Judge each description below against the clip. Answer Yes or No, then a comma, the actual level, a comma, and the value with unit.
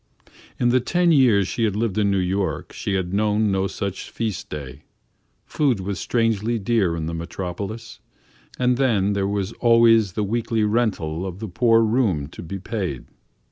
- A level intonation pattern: No, average, 3.5 semitones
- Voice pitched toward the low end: Yes, low, 105 Hz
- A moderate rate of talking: Yes, average, 175 wpm